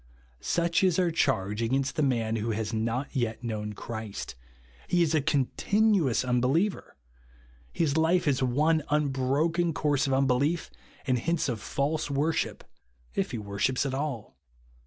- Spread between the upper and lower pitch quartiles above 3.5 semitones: Yes, average, 5.3 semitones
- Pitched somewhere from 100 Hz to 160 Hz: Yes, low, 135 Hz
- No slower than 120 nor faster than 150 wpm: Yes, average, 145 wpm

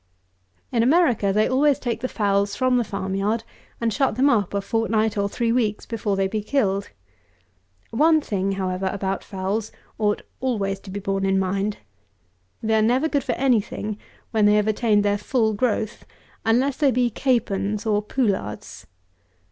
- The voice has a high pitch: Yes, high, 215 Hz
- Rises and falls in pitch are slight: No, average, 3.3 semitones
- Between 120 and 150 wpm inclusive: No, average, 170 wpm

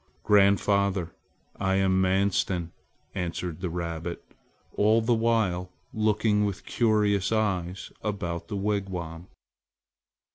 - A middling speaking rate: No, slow, 100 wpm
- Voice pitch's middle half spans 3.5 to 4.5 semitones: No, average, 2.8 semitones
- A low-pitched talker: Yes, very low, 95 Hz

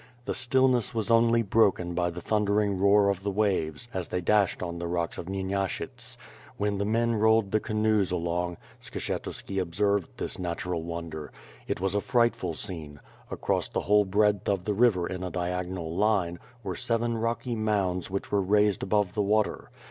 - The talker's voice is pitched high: No, low, 100 Hz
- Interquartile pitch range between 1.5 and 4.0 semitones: Yes, average, 3.2 semitones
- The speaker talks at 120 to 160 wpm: No, average, 175 wpm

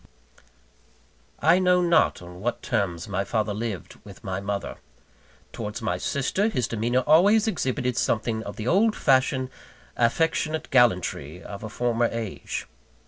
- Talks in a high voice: No, low, 120 Hz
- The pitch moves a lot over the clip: Yes, wide, 6.7 semitones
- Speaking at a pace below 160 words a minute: Yes, average, 140 wpm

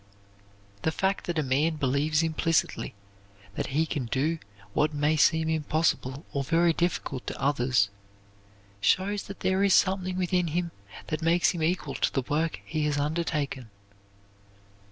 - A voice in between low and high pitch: Yes, medium, 160 Hz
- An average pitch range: Yes, average, 3.1 semitones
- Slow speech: No, average, 150 wpm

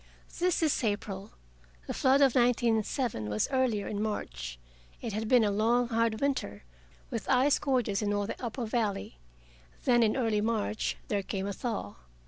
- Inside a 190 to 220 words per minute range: No, average, 165 wpm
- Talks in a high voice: Yes, high, 220 Hz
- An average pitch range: Yes, average, 3.3 semitones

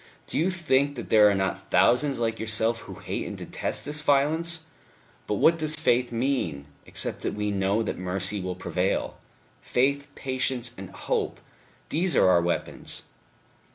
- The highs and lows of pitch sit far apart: Yes, wide, 6.3 semitones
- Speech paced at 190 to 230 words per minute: No, average, 160 wpm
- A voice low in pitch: Yes, low, 120 Hz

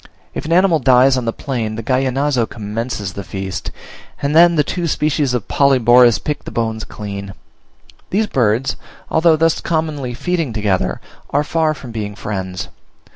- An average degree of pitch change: No, wide, 5.8 semitones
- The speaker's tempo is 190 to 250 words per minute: No, average, 160 wpm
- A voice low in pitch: Yes, low, 125 Hz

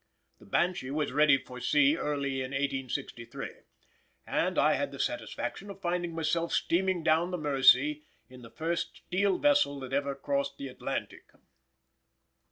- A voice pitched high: No, medium, 145 Hz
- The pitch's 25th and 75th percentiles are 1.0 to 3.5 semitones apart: No, average, 4.0 semitones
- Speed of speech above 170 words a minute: No, average, 150 wpm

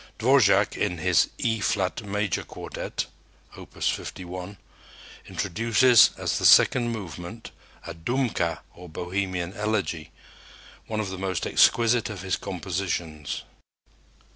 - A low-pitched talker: Yes, very low, 95 Hz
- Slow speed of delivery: Yes, slow, 115 wpm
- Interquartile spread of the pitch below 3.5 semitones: No, average, 3.8 semitones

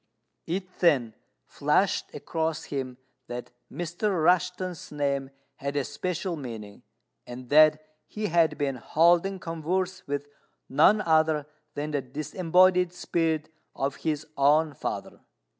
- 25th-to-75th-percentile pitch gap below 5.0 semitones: Yes, average, 3.8 semitones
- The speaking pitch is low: No, medium, 155 Hz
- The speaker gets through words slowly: Yes, slow, 120 wpm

